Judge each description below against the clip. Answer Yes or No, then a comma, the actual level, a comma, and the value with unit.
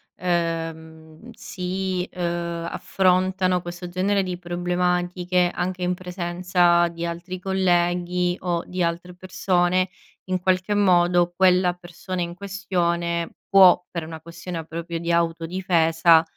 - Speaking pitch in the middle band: Yes, medium, 175 Hz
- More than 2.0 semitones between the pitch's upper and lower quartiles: No, narrow, 1.3 semitones